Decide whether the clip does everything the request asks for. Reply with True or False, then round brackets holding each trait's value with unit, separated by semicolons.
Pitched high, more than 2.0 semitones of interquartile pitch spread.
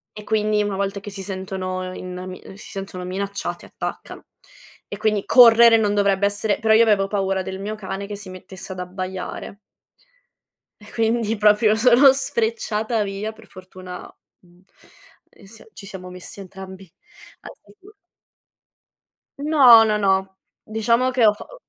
True (205 Hz; 2.5 semitones)